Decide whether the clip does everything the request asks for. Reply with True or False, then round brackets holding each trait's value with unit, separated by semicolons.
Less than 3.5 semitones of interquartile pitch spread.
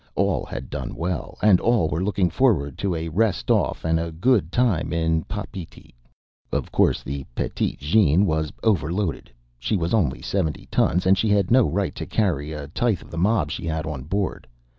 False (4.6 semitones)